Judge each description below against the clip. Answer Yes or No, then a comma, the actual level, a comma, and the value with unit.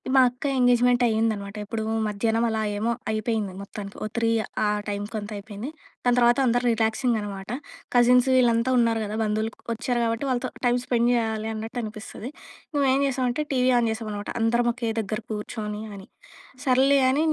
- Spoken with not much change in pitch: Yes, narrow, 2.3 semitones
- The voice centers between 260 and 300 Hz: No, high, 230 Hz